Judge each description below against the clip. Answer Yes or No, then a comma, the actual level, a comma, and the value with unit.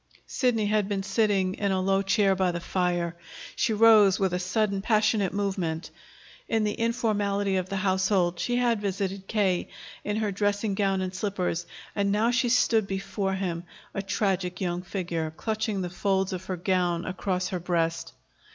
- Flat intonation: Yes, narrow, 2.2 semitones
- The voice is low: No, high, 195 Hz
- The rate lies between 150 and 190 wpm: Yes, average, 170 wpm